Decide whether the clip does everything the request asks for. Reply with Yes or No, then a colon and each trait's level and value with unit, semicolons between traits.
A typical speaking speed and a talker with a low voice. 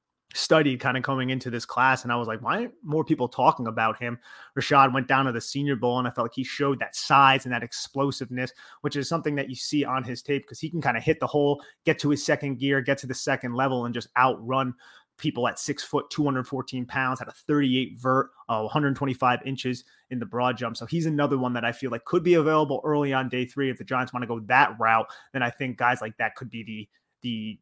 No: fast, 260 wpm; low, 130 Hz